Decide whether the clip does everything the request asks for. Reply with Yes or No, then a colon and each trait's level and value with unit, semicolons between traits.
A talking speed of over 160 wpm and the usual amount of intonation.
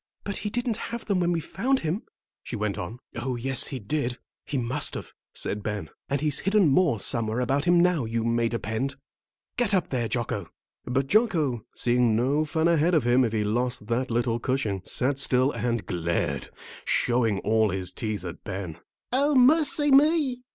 No: average, 185 wpm; wide, 7.5 semitones